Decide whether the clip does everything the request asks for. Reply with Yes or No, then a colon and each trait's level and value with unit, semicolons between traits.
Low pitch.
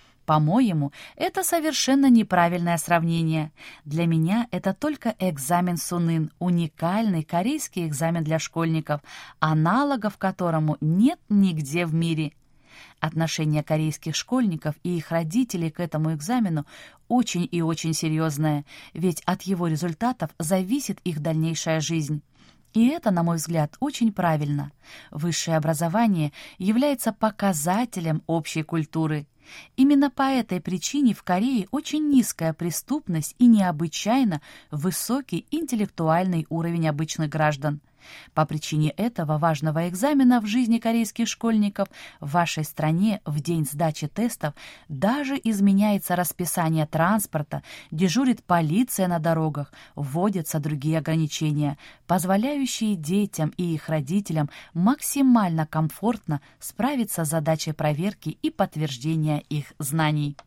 No: medium, 170 Hz